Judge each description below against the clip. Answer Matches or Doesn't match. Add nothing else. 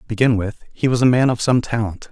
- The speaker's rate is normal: Doesn't match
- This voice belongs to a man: Matches